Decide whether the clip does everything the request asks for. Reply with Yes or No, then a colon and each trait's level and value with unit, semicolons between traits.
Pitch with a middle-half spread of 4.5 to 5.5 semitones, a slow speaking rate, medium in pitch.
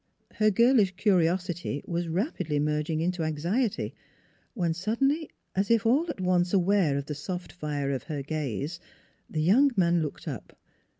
No: average, 4.8 semitones; average, 155 wpm; medium, 175 Hz